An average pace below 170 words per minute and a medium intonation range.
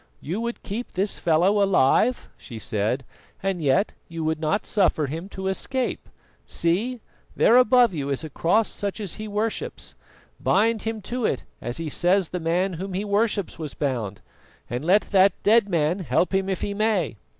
No: average, 180 wpm; average, 4.9 semitones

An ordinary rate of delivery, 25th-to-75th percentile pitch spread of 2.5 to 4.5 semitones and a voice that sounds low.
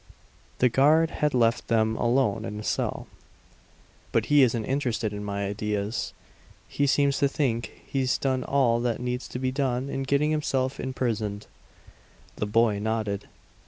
Yes: average, 155 wpm; average, 3.7 semitones; low, 125 Hz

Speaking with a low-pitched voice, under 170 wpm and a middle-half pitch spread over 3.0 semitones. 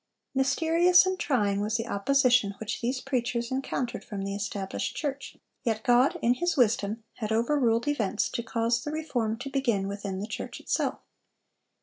No: high, 235 Hz; average, 160 wpm; average, 4.3 semitones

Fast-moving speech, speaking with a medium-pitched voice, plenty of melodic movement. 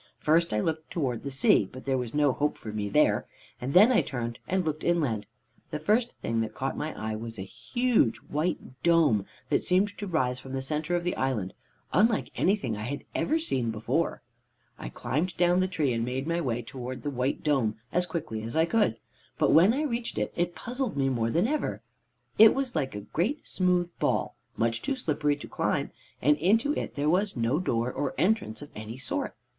Yes: fast, 210 wpm; medium, 150 Hz; wide, 6.8 semitones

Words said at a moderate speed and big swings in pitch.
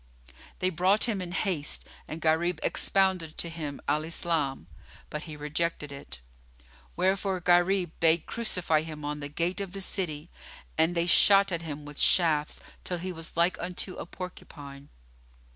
No: average, 160 wpm; average, 3.2 semitones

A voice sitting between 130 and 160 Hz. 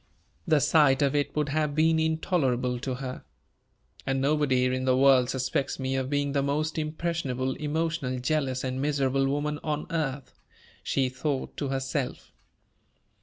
Yes: medium, 140 Hz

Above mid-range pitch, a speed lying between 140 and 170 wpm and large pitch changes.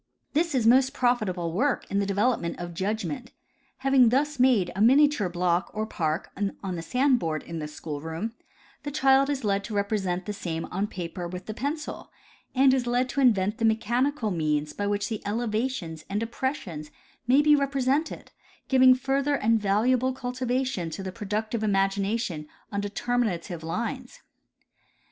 Yes: high, 220 Hz; average, 165 wpm; wide, 5.7 semitones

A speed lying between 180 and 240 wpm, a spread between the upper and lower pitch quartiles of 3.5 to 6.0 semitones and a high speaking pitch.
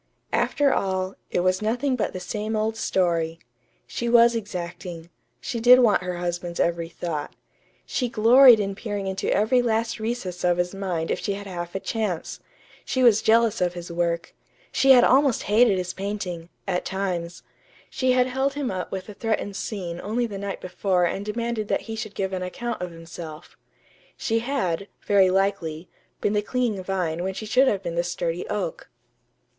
Yes: average, 185 wpm; average, 4.5 semitones; high, 195 Hz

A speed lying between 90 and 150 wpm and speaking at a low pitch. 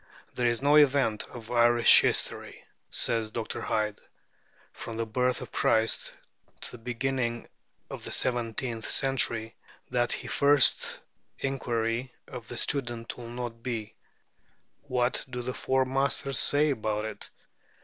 Yes: slow, 135 wpm; low, 120 Hz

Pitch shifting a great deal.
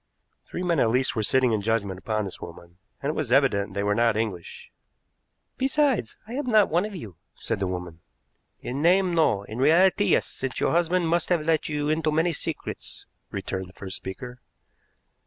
Yes: wide, 8.8 semitones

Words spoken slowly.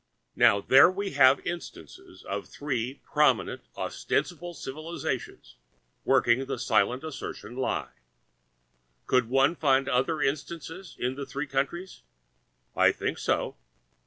Yes: slow, 115 wpm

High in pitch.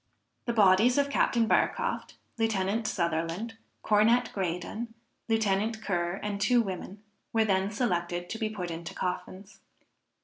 Yes: high, 210 Hz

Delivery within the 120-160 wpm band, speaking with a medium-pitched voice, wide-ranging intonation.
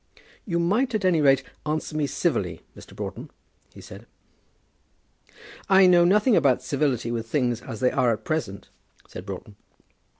Yes: average, 155 wpm; medium, 145 Hz; wide, 7.0 semitones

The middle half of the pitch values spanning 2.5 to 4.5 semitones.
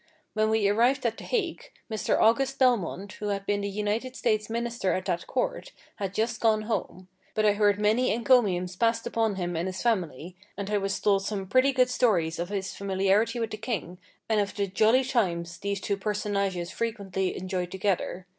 Yes: average, 3.2 semitones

